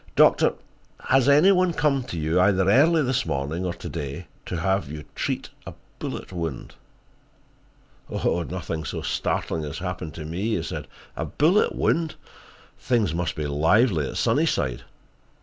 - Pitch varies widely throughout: Yes, wide, 8.8 semitones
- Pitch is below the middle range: Yes, very low, 90 Hz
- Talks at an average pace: Yes, average, 150 wpm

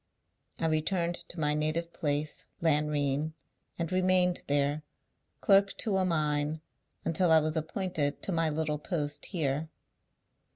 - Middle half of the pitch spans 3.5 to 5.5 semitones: No, narrow, 2.6 semitones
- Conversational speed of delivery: No, slow, 130 wpm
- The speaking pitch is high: No, medium, 155 Hz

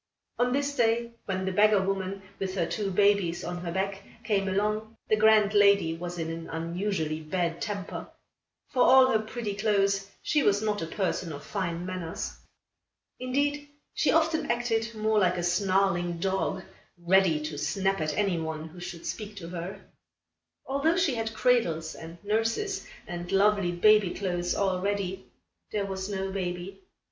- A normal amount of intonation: Yes, average, 3.5 semitones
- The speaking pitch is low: No, high, 195 Hz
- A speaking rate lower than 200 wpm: Yes, average, 165 wpm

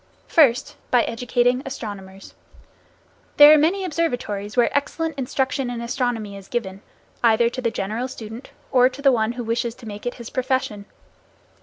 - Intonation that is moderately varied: Yes, average, 3.0 semitones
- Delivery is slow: No, average, 155 wpm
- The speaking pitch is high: Yes, high, 245 Hz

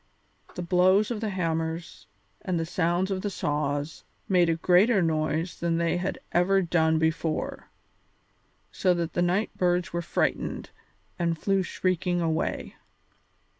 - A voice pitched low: No, medium, 175 Hz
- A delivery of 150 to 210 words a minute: No, average, 140 wpm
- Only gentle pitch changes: Yes, narrow, 2.2 semitones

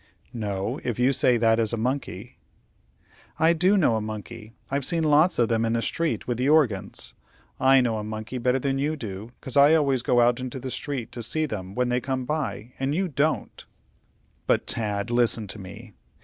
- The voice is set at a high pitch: No, low, 125 Hz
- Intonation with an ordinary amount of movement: Yes, average, 3.9 semitones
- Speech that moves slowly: No, fast, 205 wpm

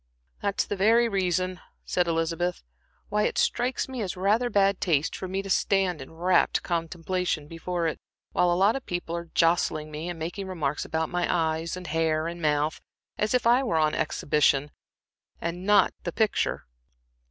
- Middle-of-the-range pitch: Yes, medium, 175 Hz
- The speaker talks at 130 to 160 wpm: No, average, 185 wpm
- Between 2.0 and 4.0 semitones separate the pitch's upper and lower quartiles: Yes, average, 3.2 semitones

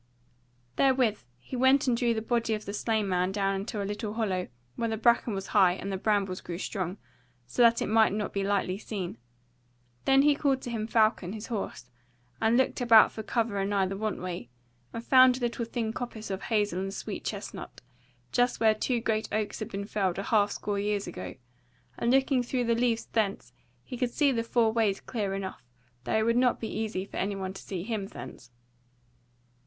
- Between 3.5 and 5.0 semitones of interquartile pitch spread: No, average, 3.1 semitones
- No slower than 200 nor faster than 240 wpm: Yes, fast, 205 wpm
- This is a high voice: Yes, high, 215 Hz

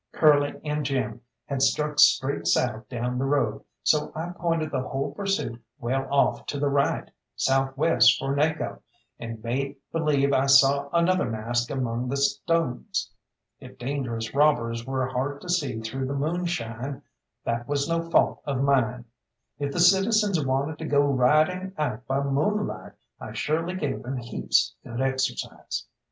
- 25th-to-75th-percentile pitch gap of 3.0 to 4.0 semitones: Yes, average, 3.3 semitones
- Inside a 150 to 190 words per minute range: Yes, average, 155 wpm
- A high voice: No, medium, 140 Hz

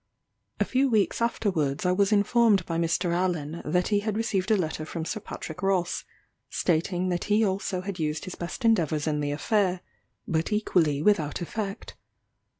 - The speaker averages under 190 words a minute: Yes, average, 170 wpm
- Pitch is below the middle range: No, medium, 185 Hz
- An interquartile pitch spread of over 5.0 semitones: No, average, 4.1 semitones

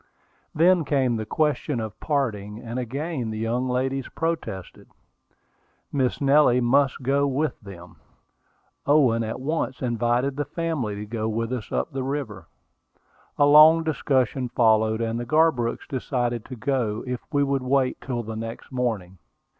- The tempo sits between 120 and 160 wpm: Yes, average, 150 wpm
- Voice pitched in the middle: No, low, 125 Hz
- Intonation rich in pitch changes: No, average, 3.9 semitones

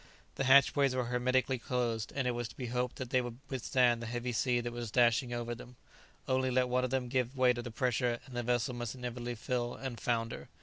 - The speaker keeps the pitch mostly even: Yes, narrow, 1.2 semitones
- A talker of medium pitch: No, low, 125 Hz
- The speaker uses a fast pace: Yes, fast, 230 wpm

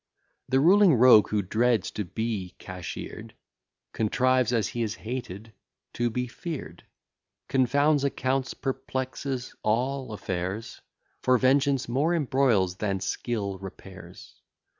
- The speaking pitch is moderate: No, low, 120 Hz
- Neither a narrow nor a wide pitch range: Yes, average, 4.5 semitones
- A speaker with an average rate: No, slow, 115 wpm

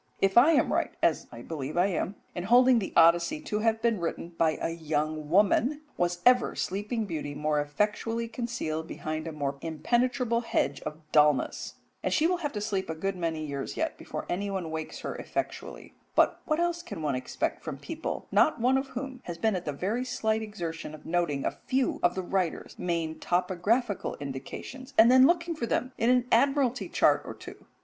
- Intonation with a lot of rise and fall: Yes, wide, 7.3 semitones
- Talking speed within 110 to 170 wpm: No, average, 195 wpm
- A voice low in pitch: No, high, 195 Hz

